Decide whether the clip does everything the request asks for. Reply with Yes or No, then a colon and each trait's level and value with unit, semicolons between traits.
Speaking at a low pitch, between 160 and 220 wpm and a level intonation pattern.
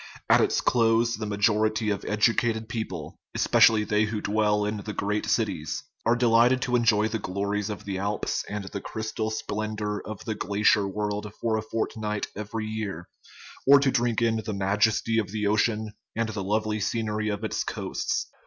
Yes: low, 110 Hz; average, 175 wpm; narrow, 1.3 semitones